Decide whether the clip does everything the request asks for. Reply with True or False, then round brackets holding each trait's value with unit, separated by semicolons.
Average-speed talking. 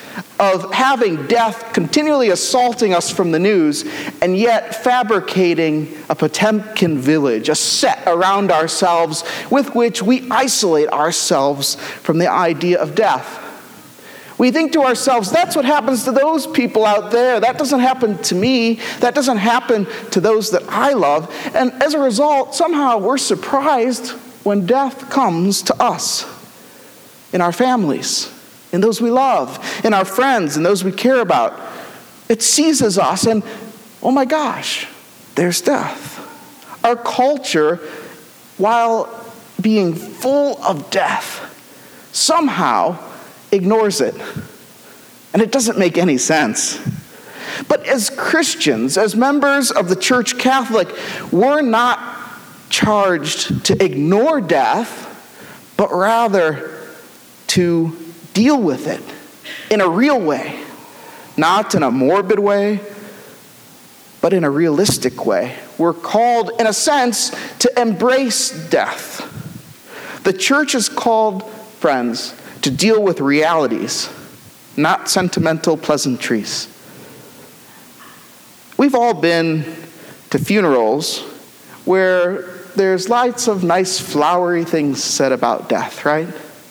False (120 wpm)